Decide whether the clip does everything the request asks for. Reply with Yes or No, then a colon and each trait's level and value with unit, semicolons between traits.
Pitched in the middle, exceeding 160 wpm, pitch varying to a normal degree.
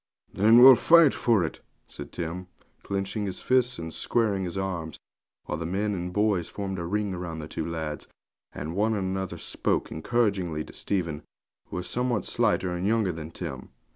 No: very low, 95 Hz; average, 180 wpm; average, 4.1 semitones